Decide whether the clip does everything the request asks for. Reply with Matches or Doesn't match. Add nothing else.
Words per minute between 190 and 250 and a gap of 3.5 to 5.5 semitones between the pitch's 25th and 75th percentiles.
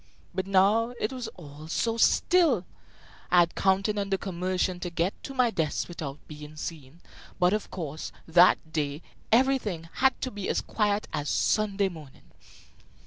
Doesn't match